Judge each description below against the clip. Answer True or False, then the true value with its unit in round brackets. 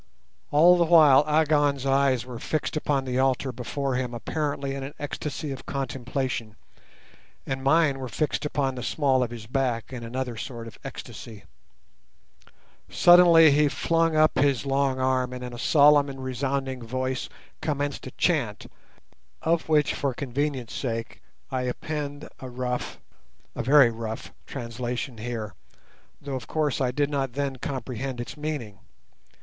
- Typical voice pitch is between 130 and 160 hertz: True (135 Hz)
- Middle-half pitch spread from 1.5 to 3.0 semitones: True (2.7 semitones)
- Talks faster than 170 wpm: False (150 wpm)